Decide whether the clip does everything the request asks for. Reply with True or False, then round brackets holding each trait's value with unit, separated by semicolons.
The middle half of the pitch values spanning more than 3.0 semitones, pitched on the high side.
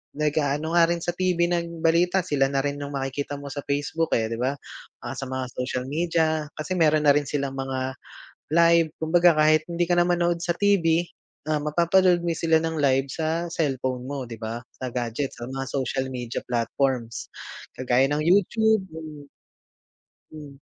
False (4.0 semitones; 150 Hz)